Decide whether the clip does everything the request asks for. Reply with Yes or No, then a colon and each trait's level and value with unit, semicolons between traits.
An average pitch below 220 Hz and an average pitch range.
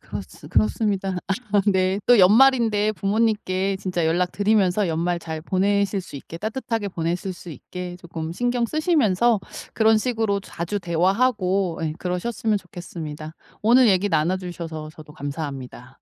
Yes: medium, 185 Hz; average, 4.1 semitones